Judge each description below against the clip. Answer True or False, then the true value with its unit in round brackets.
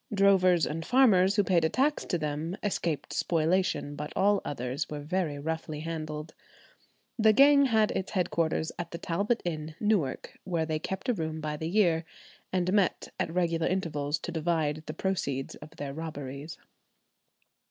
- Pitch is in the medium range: True (165 Hz)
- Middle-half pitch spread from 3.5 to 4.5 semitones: True (3.8 semitones)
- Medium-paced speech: True (165 wpm)